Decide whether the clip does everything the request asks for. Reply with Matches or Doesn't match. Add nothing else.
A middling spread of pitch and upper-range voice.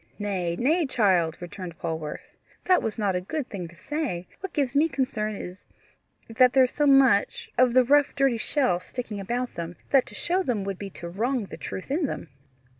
Doesn't match